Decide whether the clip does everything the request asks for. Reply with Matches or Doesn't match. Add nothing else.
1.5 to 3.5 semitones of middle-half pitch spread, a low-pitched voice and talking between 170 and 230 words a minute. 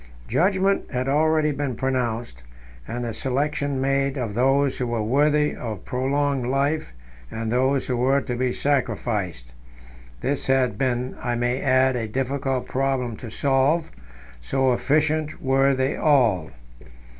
Doesn't match